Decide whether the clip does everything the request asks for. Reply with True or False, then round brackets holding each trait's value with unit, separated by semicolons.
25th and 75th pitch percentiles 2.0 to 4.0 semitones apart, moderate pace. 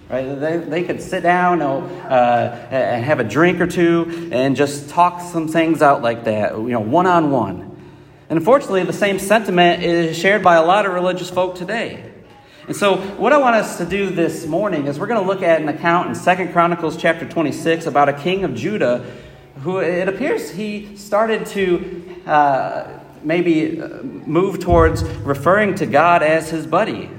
True (3.7 semitones; 190 wpm)